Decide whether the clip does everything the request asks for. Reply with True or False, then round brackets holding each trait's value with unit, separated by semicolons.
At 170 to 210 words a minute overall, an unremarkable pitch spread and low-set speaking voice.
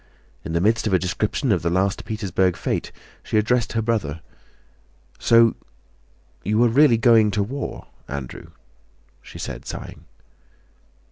False (145 wpm; 4.0 semitones; 105 Hz)